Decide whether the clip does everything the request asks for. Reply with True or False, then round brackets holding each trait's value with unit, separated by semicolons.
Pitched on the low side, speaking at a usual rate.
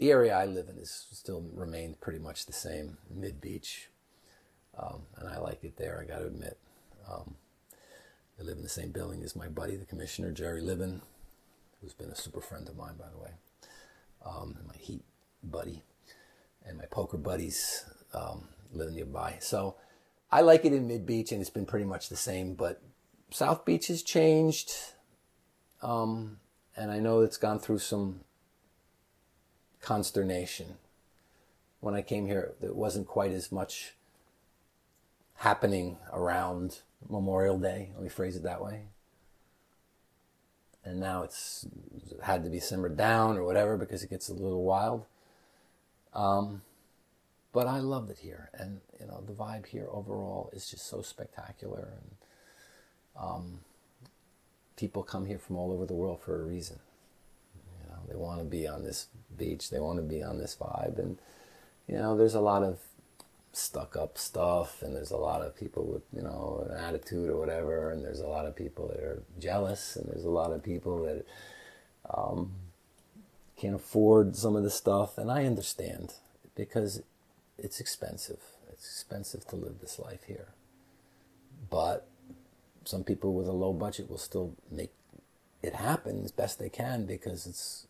True (95 Hz; 165 wpm)